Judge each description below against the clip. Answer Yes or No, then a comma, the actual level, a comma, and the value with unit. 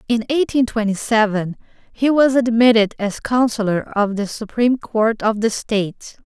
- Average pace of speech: Yes, average, 155 wpm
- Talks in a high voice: Yes, high, 225 Hz